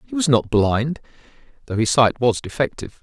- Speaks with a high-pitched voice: No, low, 125 Hz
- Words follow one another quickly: No, average, 180 wpm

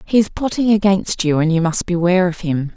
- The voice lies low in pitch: No, medium, 185 Hz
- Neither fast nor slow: No, fast, 240 wpm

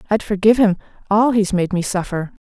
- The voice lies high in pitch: Yes, high, 200 Hz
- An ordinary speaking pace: Yes, average, 195 wpm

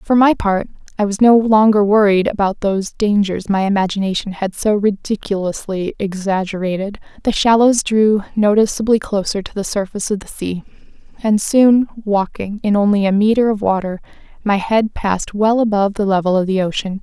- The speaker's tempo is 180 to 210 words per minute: No, average, 165 wpm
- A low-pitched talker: No, high, 205 Hz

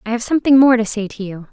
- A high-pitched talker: Yes, high, 230 Hz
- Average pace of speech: No, fast, 315 wpm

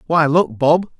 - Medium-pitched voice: Yes, medium, 160 Hz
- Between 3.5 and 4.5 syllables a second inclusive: Yes, 3.8 syllables/s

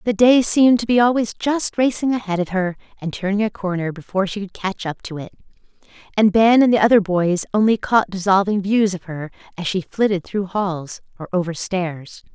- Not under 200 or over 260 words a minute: Yes, fast, 205 wpm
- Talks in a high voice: Yes, high, 200 Hz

